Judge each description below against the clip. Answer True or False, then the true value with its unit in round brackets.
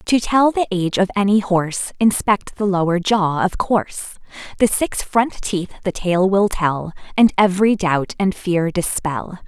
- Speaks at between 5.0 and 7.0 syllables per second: False (4.4 syllables/s)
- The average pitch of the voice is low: False (195 Hz)